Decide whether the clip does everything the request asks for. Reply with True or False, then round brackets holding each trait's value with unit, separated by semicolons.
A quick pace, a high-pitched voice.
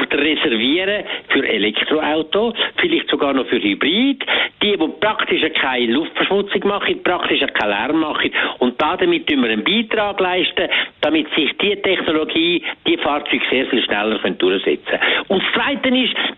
False (150 wpm; 235 Hz)